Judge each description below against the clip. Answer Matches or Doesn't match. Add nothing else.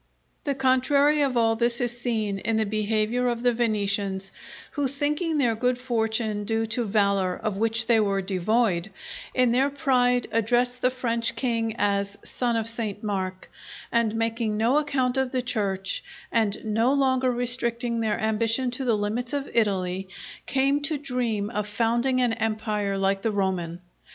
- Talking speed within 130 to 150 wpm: Doesn't match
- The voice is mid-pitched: Doesn't match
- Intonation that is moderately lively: Matches